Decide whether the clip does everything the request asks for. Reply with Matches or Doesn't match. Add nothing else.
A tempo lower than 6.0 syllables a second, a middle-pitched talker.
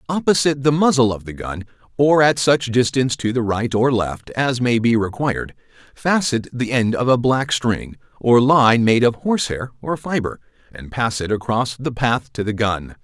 Doesn't match